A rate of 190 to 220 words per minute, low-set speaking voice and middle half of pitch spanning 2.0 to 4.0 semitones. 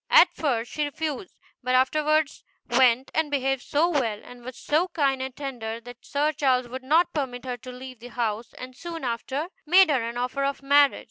No: average, 200 wpm; very high, 265 Hz; average, 3.3 semitones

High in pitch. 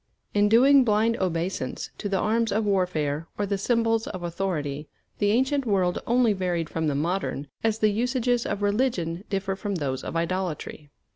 Yes: high, 195 Hz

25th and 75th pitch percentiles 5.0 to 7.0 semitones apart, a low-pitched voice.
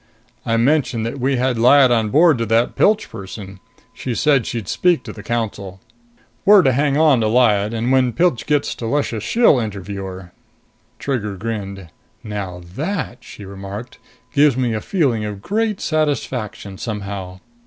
Yes: wide, 5.5 semitones; low, 115 Hz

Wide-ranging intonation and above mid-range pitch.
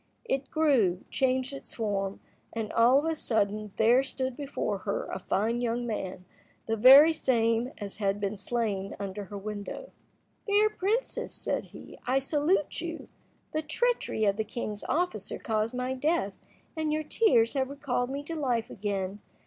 Yes: wide, 5.7 semitones; high, 240 Hz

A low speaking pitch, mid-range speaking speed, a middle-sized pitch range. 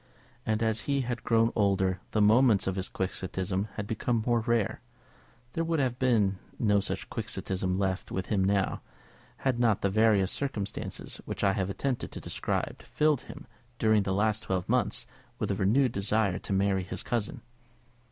Yes: low, 105 Hz; average, 170 wpm; average, 3.5 semitones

